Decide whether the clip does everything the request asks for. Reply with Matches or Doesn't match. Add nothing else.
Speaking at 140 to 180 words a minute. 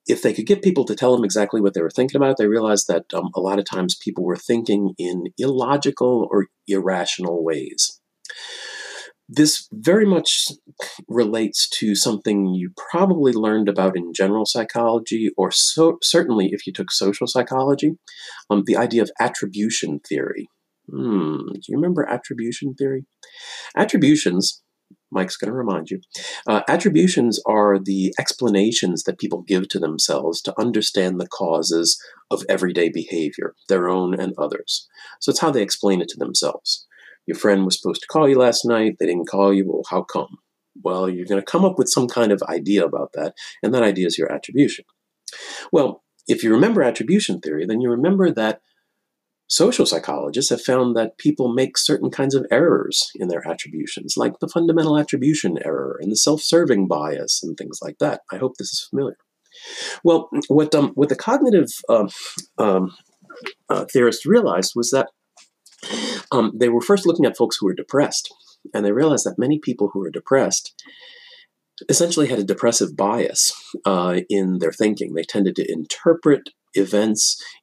Matches